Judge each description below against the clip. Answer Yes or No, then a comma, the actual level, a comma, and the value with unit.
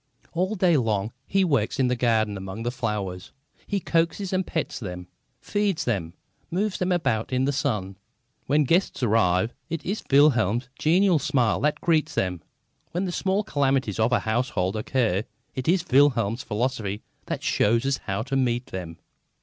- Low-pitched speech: Yes, low, 125 Hz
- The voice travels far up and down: Yes, wide, 7.1 semitones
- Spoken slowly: No, average, 165 wpm